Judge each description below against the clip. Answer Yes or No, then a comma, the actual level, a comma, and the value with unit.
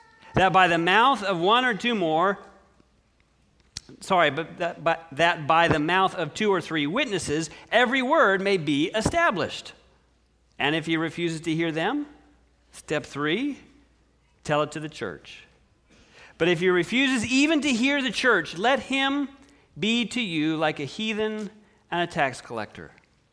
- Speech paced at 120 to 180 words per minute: Yes, average, 160 wpm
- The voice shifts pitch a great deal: Yes, wide, 6.9 semitones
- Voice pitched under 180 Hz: No, medium, 185 Hz